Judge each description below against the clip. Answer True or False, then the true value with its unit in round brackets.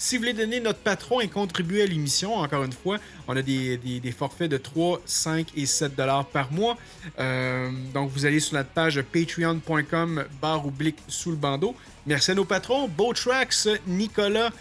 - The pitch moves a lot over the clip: True (6.6 semitones)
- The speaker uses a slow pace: False (190 wpm)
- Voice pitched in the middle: True (160 Hz)